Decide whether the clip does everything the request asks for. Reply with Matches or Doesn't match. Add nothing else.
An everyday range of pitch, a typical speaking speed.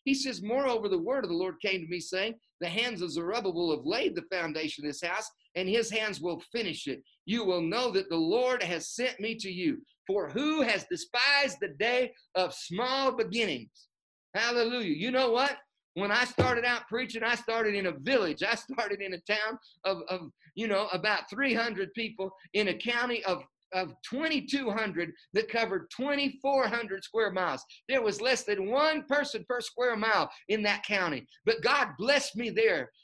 Matches